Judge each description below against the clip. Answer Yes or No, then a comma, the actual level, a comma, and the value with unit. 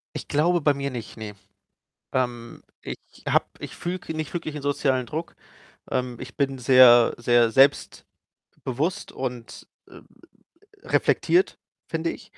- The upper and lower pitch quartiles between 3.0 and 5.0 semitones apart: Yes, average, 3.6 semitones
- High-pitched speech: No, low, 130 Hz